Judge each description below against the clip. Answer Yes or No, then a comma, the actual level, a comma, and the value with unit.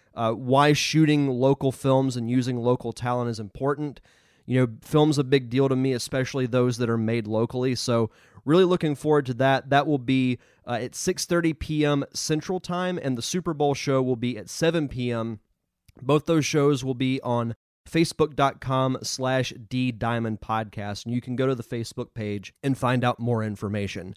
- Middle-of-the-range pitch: No, low, 130 Hz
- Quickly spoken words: No, average, 180 wpm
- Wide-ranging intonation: No, average, 3.4 semitones